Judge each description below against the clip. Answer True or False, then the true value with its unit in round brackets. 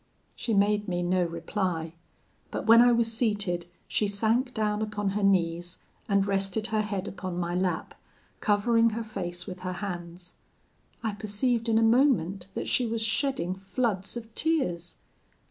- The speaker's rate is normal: True (160 wpm)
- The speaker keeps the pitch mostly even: False (3.7 semitones)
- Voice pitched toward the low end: False (205 Hz)